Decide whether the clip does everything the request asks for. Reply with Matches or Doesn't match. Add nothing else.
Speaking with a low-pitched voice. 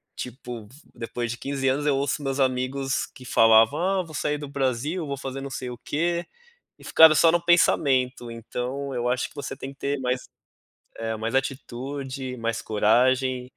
Matches